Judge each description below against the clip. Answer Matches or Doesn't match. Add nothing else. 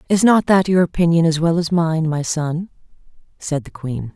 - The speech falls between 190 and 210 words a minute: Matches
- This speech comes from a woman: Matches